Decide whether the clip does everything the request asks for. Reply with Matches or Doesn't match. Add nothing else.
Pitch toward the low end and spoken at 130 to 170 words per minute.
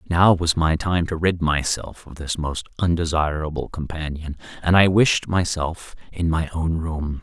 Matches